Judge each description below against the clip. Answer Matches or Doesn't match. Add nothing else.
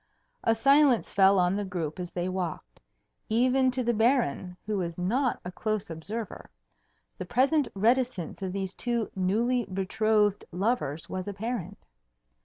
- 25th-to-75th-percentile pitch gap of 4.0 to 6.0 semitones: Matches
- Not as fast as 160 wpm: Matches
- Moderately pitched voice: Doesn't match